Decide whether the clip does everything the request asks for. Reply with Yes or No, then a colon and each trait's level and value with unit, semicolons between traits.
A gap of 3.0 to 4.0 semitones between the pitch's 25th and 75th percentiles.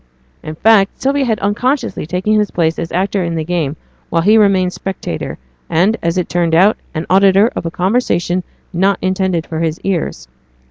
Yes: average, 3.3 semitones